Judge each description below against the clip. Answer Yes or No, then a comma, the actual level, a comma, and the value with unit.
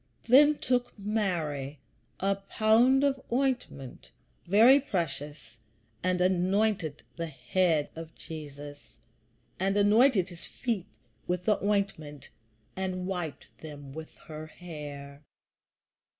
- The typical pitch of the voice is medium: Yes, medium, 180 Hz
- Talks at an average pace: No, slow, 105 wpm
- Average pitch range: No, wide, 5.8 semitones